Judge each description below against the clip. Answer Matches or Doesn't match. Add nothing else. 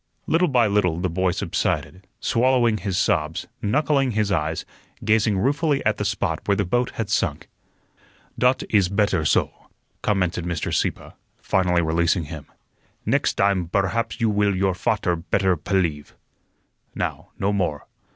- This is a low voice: Matches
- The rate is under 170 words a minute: Matches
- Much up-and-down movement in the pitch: Doesn't match